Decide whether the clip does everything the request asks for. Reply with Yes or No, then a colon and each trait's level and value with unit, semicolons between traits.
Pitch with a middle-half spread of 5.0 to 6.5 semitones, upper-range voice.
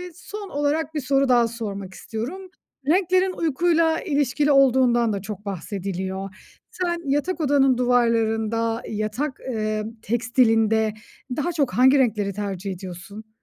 Yes: average, 5.3 semitones; high, 240 Hz